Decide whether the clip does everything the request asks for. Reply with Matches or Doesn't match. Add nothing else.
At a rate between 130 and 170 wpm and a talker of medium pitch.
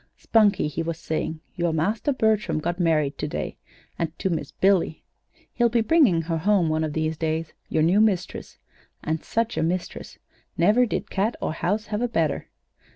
Doesn't match